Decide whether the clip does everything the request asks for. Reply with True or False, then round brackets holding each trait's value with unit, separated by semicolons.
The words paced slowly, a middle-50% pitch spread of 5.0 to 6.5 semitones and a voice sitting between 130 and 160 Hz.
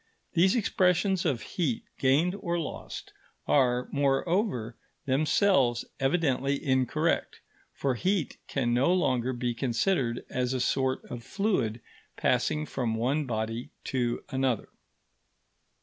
True (115 wpm; 5.6 semitones; 135 Hz)